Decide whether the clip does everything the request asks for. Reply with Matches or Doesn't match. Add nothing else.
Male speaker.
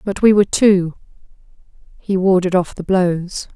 Doesn't match